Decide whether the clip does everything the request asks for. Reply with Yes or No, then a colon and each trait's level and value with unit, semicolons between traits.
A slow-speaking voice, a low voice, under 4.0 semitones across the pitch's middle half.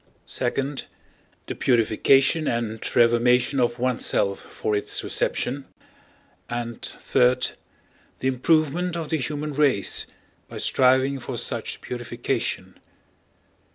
Yes: slow, 100 wpm; low, 125 Hz; average, 2.8 semitones